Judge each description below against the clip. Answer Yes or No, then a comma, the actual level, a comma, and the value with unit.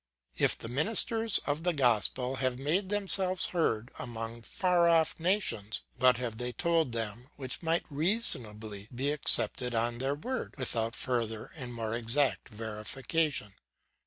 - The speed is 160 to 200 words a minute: No, average, 140 wpm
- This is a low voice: Yes, low, 130 Hz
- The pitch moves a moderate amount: No, wide, 6.2 semitones